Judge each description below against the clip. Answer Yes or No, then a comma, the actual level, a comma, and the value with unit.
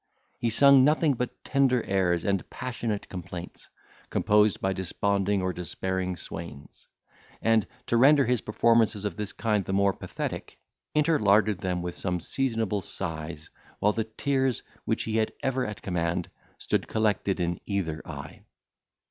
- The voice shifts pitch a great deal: No, average, 4.2 semitones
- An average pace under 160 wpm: Yes, average, 145 wpm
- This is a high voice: No, low, 105 Hz